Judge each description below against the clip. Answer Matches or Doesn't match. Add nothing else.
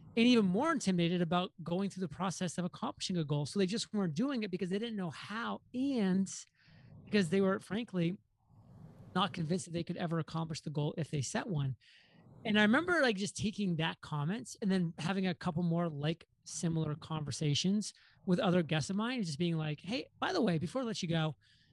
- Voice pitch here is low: Doesn't match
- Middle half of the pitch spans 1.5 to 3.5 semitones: Doesn't match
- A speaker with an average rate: Doesn't match